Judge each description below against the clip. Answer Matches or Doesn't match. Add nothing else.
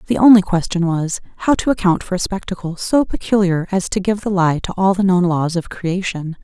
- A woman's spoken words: Matches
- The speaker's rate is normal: Doesn't match